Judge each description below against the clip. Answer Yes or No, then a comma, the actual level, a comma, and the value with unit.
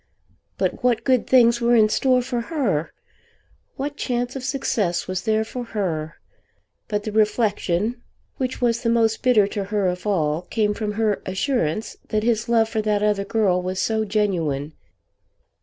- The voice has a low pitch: No, high, 215 Hz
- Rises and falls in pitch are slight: No, average, 3.4 semitones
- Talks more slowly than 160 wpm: No, average, 165 wpm